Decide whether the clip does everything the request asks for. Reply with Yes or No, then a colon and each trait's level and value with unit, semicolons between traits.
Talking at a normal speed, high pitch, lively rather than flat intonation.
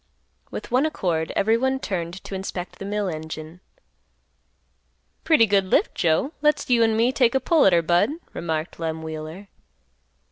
Yes: average, 155 wpm; high, 195 Hz; wide, 6.1 semitones